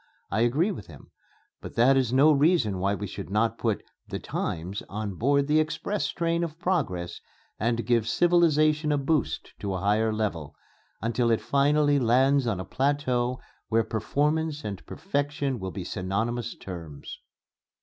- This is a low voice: Yes, low, 125 Hz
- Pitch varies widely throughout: Yes, wide, 6.0 semitones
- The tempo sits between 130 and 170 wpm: Yes, average, 160 wpm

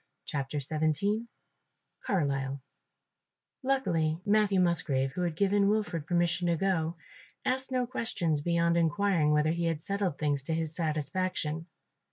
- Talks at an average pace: No, slow, 130 wpm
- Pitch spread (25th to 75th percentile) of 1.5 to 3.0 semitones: No, average, 4.5 semitones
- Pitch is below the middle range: No, medium, 170 Hz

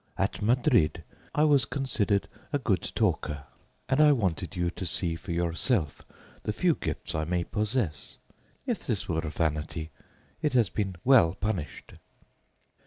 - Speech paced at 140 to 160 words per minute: Yes, average, 145 wpm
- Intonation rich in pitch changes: Yes, wide, 7.3 semitones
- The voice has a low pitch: Yes, very low, 95 Hz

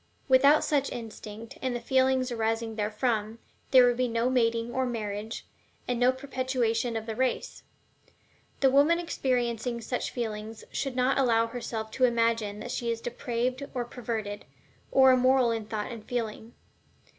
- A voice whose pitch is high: Yes, high, 240 Hz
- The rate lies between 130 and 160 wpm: Yes, average, 155 wpm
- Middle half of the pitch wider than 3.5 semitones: No, narrow, 2.4 semitones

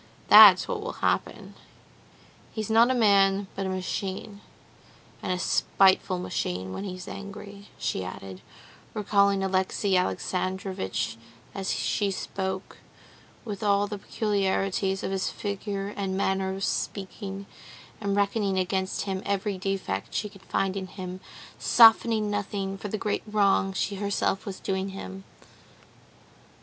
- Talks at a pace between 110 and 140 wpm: Yes, slow, 135 wpm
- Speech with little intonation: Yes, narrow, 1.2 semitones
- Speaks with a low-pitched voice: No, high, 195 Hz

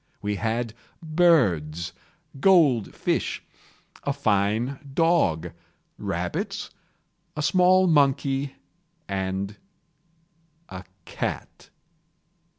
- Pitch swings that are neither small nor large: No, wide, 8.1 semitones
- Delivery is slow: Yes, slow, 70 wpm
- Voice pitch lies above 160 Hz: No, low, 120 Hz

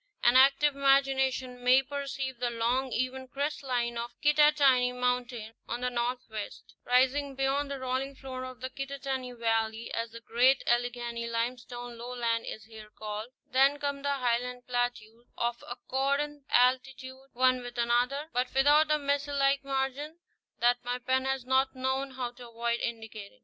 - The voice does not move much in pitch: Yes, narrow, 2.1 semitones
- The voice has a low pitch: No, very high, 255 Hz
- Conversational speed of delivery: Yes, average, 160 wpm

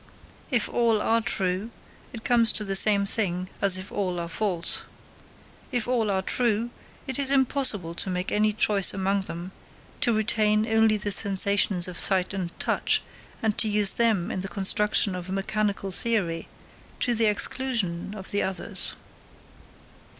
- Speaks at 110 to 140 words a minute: No, average, 160 wpm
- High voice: Yes, high, 205 Hz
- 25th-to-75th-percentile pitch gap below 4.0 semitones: Yes, average, 2.7 semitones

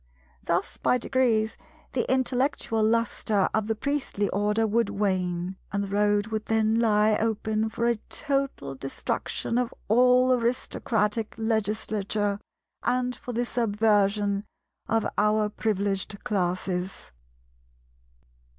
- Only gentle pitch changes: Yes, narrow, 2.3 semitones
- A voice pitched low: No, high, 215 Hz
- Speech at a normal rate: No, slow, 115 wpm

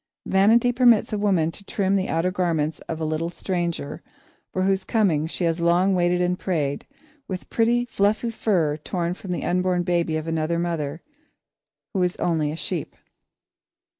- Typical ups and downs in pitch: Yes, average, 3.1 semitones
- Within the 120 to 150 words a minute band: No, average, 165 wpm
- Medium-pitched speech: Yes, medium, 180 Hz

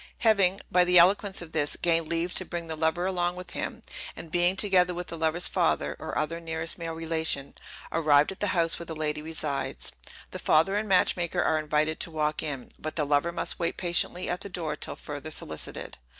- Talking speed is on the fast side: Yes, fast, 210 wpm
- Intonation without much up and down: Yes, narrow, 2.3 semitones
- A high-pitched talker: No, medium, 165 Hz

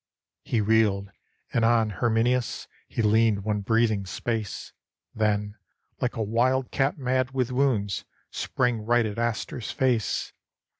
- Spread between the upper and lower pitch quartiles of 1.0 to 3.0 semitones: Yes, average, 2.7 semitones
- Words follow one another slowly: Yes, slow, 130 wpm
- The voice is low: Yes, low, 115 Hz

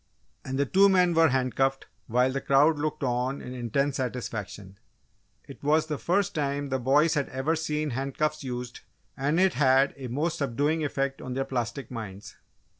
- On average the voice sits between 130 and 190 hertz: Yes, low, 135 Hz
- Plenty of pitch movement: No, average, 3.0 semitones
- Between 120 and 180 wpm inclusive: Yes, average, 175 wpm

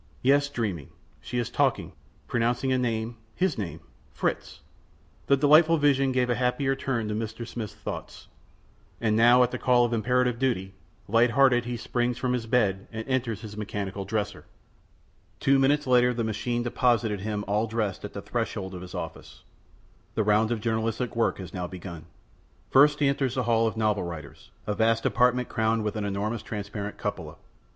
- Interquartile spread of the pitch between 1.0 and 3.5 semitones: Yes, average, 3.0 semitones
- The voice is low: Yes, low, 115 Hz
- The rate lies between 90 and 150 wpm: No, average, 180 wpm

